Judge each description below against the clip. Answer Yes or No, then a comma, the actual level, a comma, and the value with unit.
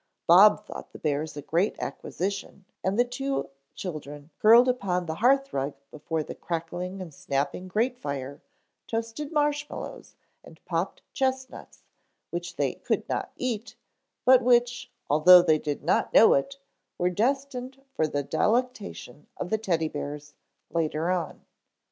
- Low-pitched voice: No, medium, 185 Hz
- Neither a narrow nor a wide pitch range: No, wide, 7.8 semitones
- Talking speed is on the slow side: No, average, 145 wpm